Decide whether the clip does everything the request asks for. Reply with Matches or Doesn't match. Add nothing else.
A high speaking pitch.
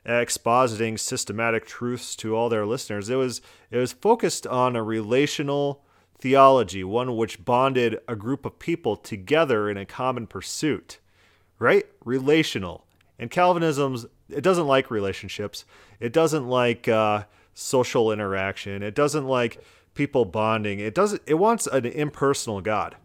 Doesn't match